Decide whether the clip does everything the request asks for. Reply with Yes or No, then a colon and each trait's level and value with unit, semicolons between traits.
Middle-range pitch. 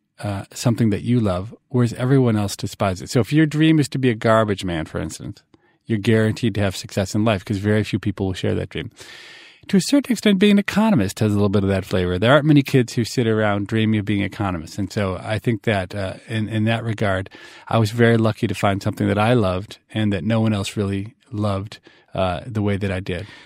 No: low, 110 Hz